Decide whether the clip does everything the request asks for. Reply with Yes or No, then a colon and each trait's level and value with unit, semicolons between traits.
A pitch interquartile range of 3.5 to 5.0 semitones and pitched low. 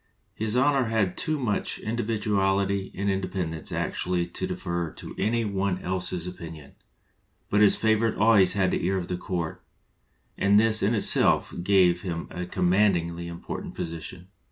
No: average, 3.1 semitones; very low, 95 Hz